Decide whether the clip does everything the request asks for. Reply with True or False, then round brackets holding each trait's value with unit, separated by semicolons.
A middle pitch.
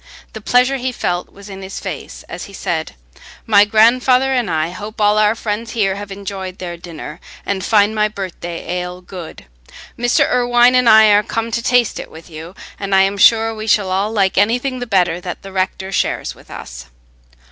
False (205 Hz)